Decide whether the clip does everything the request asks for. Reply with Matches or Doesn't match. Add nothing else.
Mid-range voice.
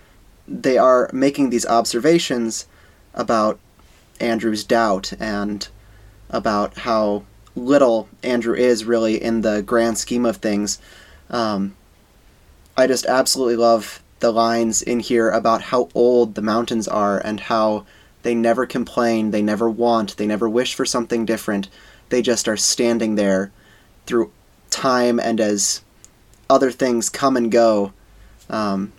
Doesn't match